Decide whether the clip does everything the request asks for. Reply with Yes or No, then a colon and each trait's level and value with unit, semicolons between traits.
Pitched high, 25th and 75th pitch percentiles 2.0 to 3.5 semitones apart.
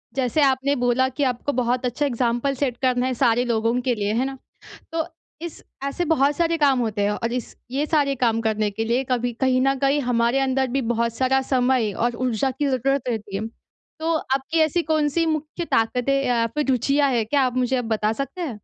Yes: very high, 255 Hz; average, 2.9 semitones